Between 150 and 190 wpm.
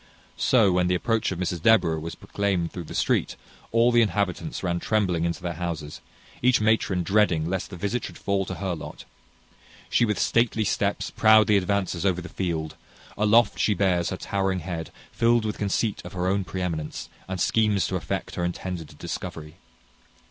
Yes: average, 180 wpm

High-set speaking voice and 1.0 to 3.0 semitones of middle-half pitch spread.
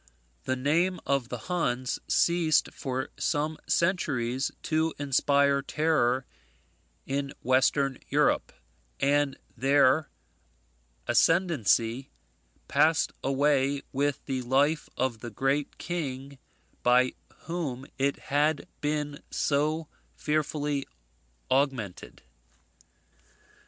No: medium, 140 Hz; narrow, 2.6 semitones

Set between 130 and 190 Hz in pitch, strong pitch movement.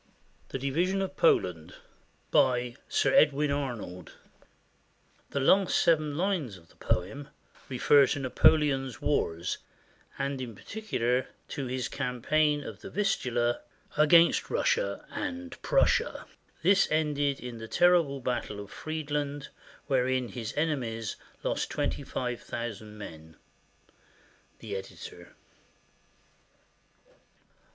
No: low, 135 Hz; average, 4.5 semitones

